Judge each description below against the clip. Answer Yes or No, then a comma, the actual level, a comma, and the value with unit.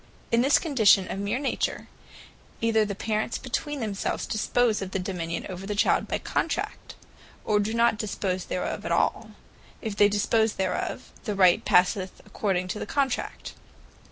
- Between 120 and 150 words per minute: No, average, 160 wpm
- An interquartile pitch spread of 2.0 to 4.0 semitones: Yes, average, 3.0 semitones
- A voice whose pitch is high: Yes, high, 210 Hz